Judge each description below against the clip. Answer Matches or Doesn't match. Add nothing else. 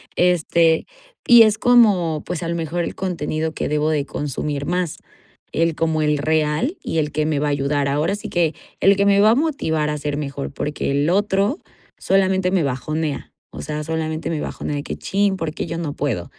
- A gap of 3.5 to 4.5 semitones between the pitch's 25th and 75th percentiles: Matches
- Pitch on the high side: Doesn't match